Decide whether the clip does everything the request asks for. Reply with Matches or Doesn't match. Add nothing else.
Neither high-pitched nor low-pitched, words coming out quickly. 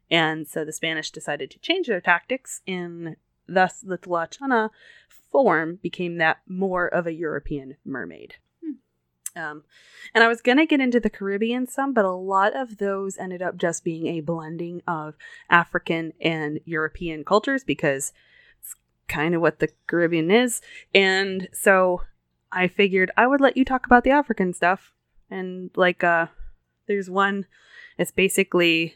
Doesn't match